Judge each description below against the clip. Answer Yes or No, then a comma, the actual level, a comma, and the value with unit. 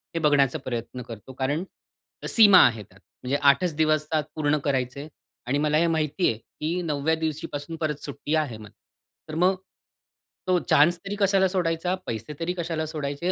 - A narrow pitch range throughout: No, average, 3.1 semitones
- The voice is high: No, medium, 155 Hz